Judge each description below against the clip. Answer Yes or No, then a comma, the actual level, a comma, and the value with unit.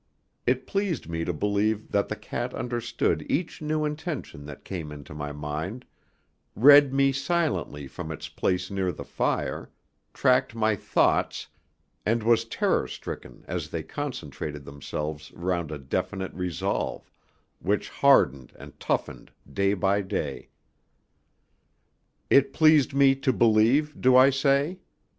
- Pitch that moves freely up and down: Yes, wide, 8.7 semitones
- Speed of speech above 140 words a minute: No, slow, 135 wpm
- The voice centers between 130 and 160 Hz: No, low, 110 Hz